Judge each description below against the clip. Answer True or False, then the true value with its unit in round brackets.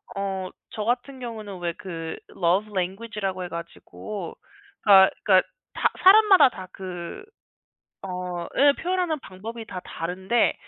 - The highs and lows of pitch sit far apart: False (4.2 semitones)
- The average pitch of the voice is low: False (195 Hz)